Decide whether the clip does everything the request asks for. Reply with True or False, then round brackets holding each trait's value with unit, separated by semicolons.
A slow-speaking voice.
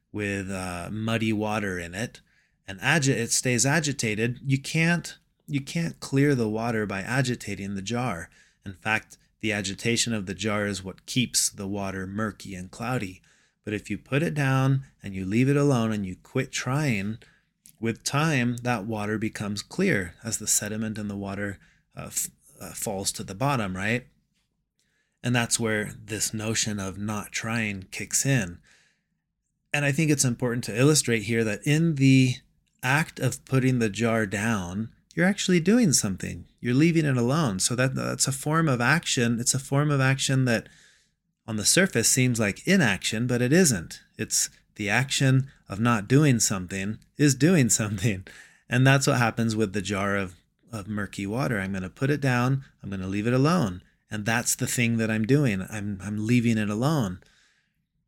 False (180 wpm)